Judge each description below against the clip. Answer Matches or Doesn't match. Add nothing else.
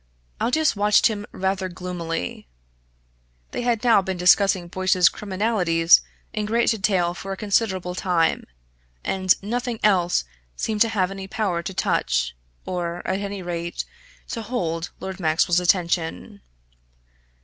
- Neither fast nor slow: Doesn't match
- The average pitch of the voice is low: Doesn't match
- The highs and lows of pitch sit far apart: Doesn't match